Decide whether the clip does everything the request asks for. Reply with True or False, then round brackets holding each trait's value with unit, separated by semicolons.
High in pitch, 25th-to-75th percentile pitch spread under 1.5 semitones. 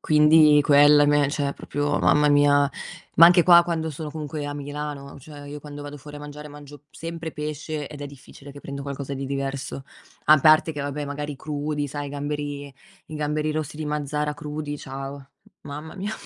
False (145 Hz; 1.0 semitones)